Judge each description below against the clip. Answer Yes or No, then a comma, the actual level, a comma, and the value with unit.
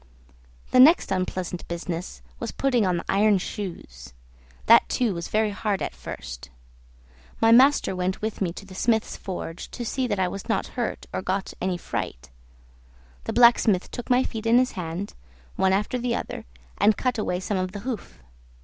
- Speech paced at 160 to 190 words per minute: Yes, average, 180 wpm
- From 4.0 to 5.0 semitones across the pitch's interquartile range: Yes, average, 4.3 semitones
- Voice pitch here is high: Yes, high, 200 Hz